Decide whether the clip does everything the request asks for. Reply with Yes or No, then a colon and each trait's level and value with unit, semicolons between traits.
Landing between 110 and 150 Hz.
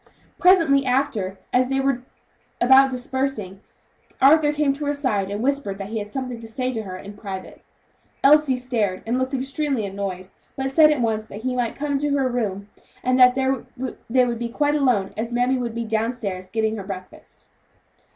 No: very high, 250 Hz